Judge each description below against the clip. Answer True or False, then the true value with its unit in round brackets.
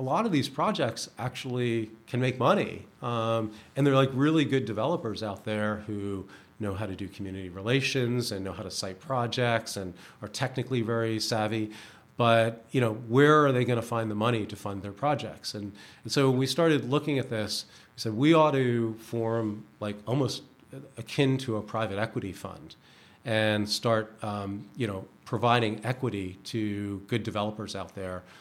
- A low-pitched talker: True (115 Hz)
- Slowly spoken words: False (180 wpm)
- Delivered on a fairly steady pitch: False (3.3 semitones)